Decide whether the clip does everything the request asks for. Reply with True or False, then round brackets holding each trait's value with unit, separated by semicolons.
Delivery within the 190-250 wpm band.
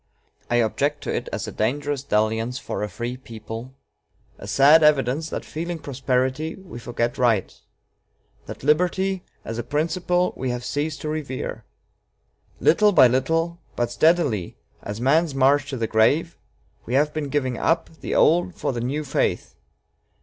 False (155 wpm)